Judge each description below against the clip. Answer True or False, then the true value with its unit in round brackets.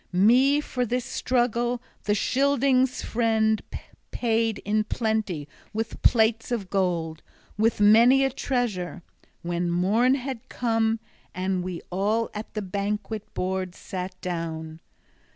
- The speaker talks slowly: True (120 wpm)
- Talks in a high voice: True (220 Hz)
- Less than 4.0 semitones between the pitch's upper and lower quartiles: False (4.6 semitones)